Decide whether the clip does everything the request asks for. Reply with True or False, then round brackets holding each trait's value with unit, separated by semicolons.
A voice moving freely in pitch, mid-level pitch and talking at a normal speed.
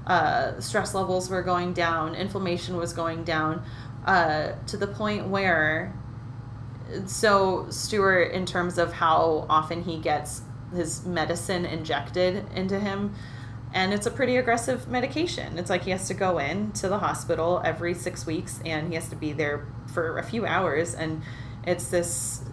True (6.4 semitones; 165 Hz; 160 wpm)